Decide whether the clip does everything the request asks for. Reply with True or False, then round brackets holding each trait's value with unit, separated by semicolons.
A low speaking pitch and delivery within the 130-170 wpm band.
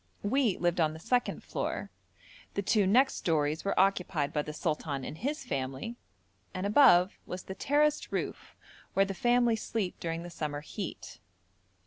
False (185 Hz; 160 wpm)